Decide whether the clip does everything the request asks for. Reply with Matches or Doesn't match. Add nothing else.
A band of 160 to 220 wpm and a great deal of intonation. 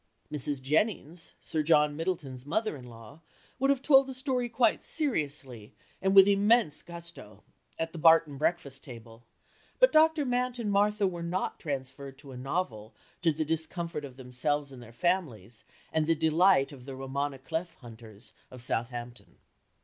Matches